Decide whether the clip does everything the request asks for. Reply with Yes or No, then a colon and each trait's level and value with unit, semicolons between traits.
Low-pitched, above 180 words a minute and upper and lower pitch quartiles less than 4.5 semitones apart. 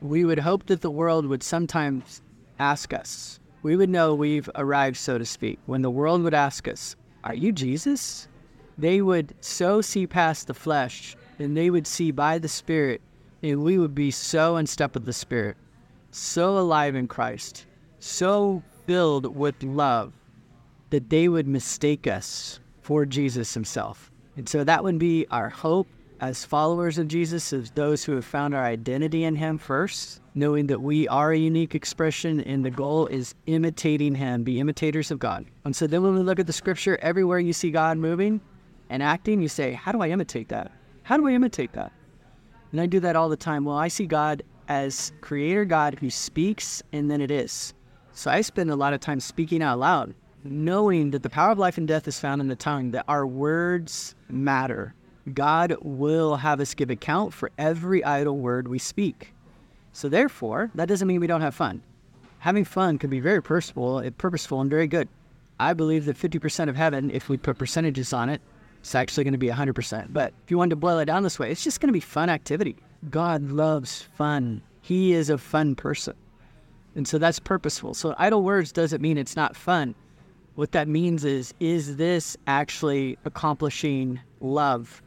No: medium, 150 Hz; average, 195 wpm; average, 3.4 semitones